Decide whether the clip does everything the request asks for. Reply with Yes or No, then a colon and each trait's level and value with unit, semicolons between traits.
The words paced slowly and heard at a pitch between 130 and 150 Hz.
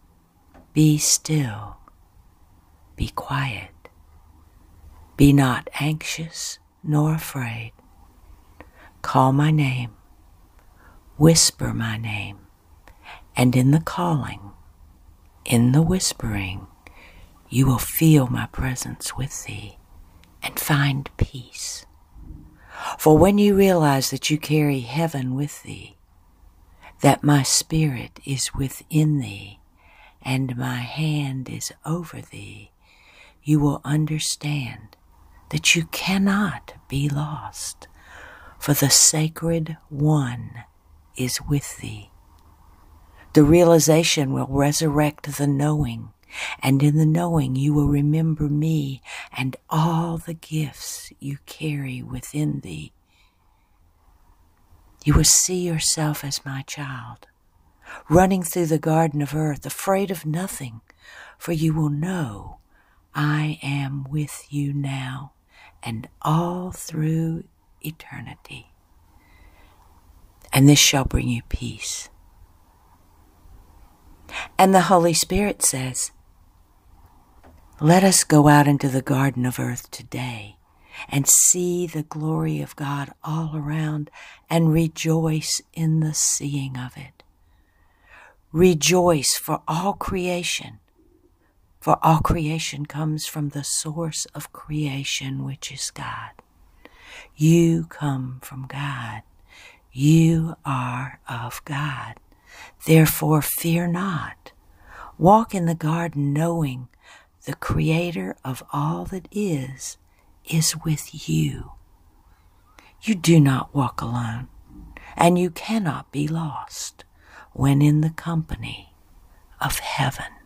Yes: slow, 105 wpm; medium, 140 Hz